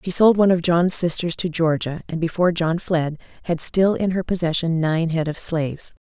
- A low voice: No, medium, 170 Hz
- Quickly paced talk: Yes, fast, 210 wpm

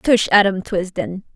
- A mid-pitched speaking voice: No, high, 195 Hz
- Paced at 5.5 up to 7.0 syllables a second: No, 4.1 syllables/s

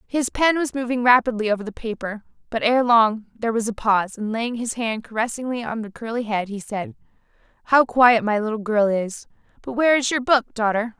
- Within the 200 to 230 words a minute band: Yes, fast, 205 wpm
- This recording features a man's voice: No, female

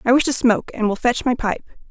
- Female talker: Yes, female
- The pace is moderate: No, fast, 285 wpm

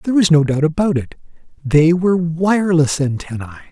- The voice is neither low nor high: Yes, medium, 160 Hz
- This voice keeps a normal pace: Yes, average, 160 wpm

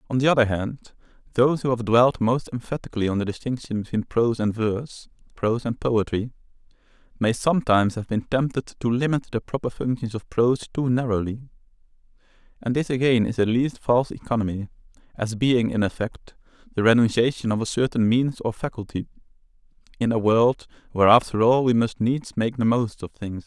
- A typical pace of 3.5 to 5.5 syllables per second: No, 5.7 syllables/s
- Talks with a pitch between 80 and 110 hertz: No, low, 120 Hz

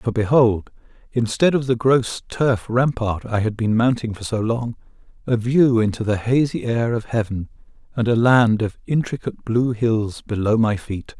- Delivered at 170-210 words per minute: Yes, average, 175 wpm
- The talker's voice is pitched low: Yes, low, 115 Hz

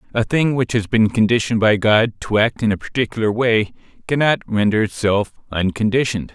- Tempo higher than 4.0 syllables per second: Yes, 5.5 syllables/s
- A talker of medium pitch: No, low, 110 Hz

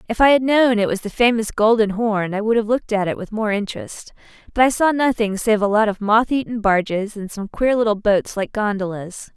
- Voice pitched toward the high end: Yes, high, 215 Hz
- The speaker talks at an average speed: No, fast, 235 wpm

